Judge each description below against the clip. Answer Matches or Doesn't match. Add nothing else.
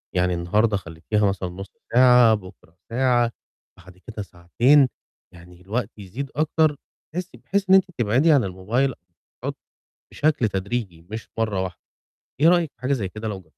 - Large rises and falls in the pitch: Matches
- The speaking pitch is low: Matches